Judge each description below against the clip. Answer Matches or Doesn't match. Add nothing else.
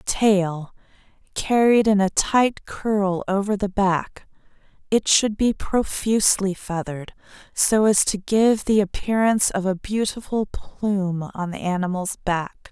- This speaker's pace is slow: Matches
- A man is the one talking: Doesn't match